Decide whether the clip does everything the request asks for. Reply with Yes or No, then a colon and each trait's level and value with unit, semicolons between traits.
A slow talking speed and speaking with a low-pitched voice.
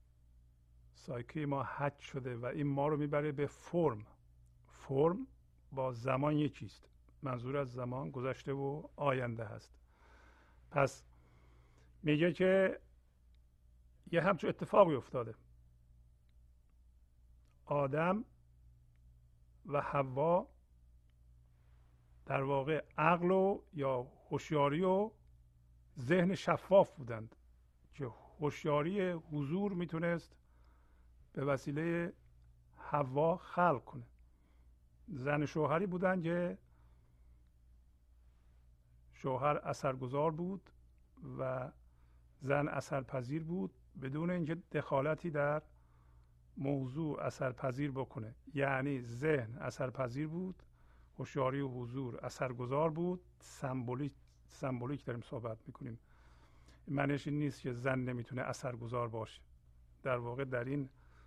Yes: slow, 95 wpm; low, 125 Hz